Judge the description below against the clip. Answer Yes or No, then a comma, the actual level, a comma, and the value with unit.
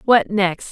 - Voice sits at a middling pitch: No, high, 200 Hz